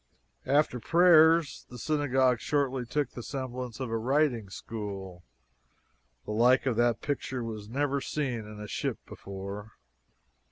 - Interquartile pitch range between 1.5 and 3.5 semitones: No, average, 4.2 semitones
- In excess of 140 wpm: No, slow, 135 wpm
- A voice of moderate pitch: No, low, 125 Hz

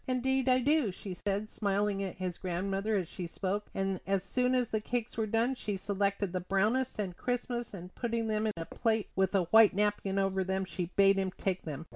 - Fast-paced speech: Yes, fast, 215 wpm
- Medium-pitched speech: No, high, 200 Hz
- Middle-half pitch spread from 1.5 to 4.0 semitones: Yes, average, 2.9 semitones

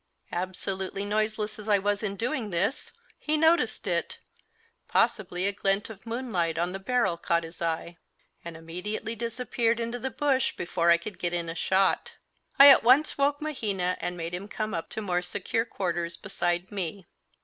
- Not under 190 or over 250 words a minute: No, average, 175 wpm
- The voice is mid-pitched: No, high, 200 Hz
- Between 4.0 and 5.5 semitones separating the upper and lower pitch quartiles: Yes, average, 4.7 semitones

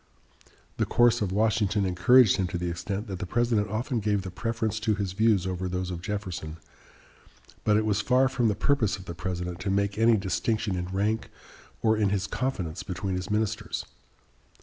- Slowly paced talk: No, average, 190 wpm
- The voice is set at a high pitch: No, low, 100 Hz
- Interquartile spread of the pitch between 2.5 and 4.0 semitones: Yes, average, 3.0 semitones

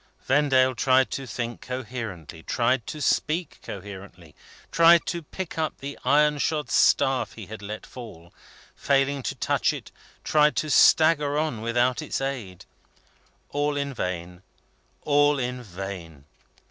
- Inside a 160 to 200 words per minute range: No, slow, 135 wpm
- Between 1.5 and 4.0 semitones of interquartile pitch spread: No, wide, 5.6 semitones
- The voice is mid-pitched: No, low, 130 Hz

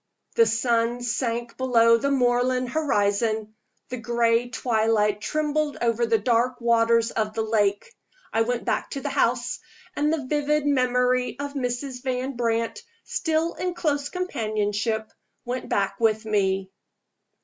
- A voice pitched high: Yes, high, 240 Hz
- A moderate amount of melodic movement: Yes, average, 3.0 semitones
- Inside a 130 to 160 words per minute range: Yes, average, 140 wpm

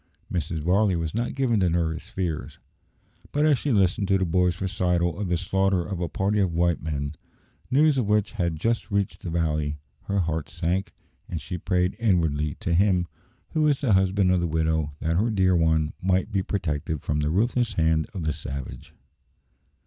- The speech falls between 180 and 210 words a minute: Yes, average, 190 wpm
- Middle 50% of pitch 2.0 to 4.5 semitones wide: Yes, average, 3.7 semitones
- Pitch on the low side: Yes, very low, 90 Hz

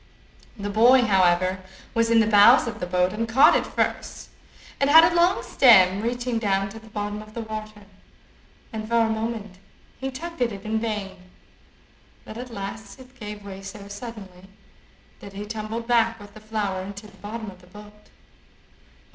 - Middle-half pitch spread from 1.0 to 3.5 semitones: Yes, narrow, 2.5 semitones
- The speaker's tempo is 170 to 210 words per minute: Yes, average, 180 wpm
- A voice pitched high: Yes, high, 215 Hz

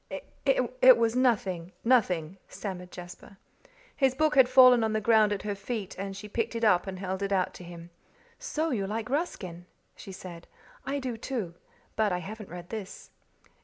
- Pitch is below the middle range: No, high, 210 Hz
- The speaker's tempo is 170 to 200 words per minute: Yes, average, 180 wpm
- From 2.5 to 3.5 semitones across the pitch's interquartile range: No, average, 4.9 semitones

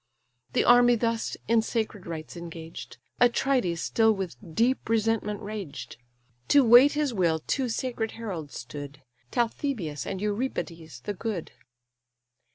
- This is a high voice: Yes, high, 215 Hz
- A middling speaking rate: No, slow, 125 wpm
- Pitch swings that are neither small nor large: No, wide, 6.2 semitones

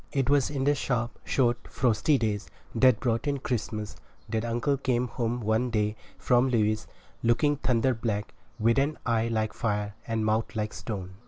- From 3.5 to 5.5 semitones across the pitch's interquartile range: No, average, 2.9 semitones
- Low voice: Yes, low, 115 Hz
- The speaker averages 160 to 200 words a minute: Yes, average, 175 wpm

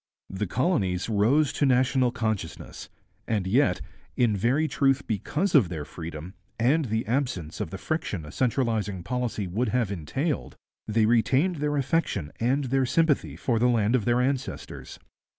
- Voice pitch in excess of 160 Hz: No, low, 120 Hz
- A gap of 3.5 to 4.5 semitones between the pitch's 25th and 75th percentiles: No, average, 5.1 semitones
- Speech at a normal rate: Yes, average, 155 wpm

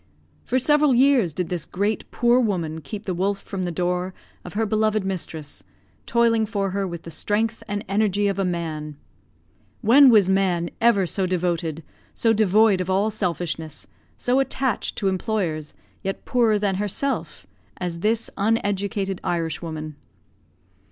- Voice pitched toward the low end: No, high, 195 Hz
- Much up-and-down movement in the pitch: No, average, 3.8 semitones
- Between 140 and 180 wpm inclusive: Yes, average, 150 wpm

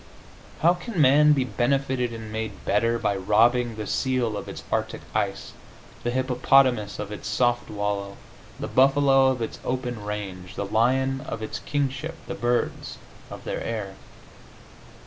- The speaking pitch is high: No, low, 120 Hz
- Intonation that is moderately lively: Yes, average, 3.8 semitones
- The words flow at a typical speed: Yes, average, 150 wpm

